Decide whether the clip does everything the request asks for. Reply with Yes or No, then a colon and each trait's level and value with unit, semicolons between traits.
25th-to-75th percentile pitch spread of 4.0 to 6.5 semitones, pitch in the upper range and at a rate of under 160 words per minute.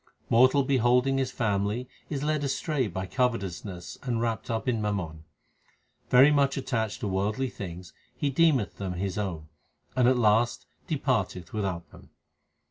No: average, 5.1 semitones; low, 115 Hz; average, 145 wpm